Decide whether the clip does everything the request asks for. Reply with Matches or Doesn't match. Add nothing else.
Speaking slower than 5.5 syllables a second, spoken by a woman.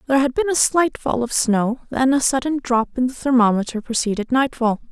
Doesn't match